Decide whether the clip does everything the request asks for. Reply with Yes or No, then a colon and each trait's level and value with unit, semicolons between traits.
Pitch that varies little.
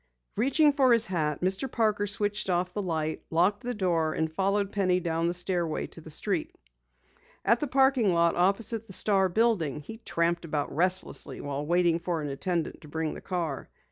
No: average, 4.1 semitones